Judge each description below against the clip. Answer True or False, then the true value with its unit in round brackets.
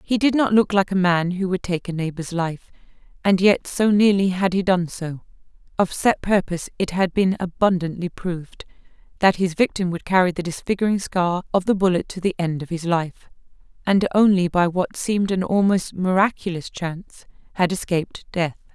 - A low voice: False (185 Hz)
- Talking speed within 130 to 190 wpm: True (185 wpm)